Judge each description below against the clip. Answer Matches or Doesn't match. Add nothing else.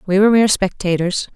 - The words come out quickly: Doesn't match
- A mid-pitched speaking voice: Doesn't match